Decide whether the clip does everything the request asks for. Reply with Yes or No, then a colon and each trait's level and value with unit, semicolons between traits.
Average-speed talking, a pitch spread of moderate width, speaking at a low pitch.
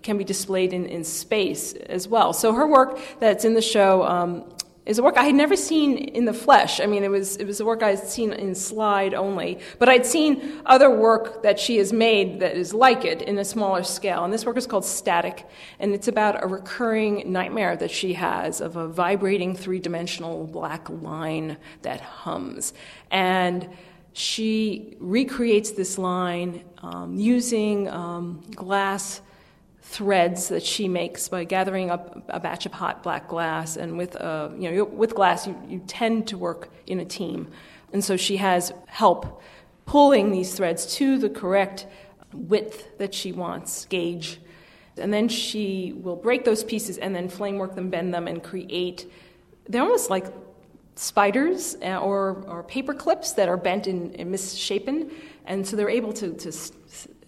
No: average, 180 wpm; average, 3.7 semitones; high, 195 Hz